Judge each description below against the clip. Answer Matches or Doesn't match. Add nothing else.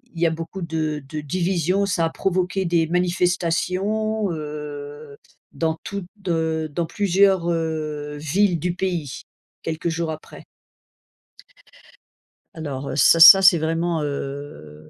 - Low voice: Doesn't match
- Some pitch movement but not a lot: Matches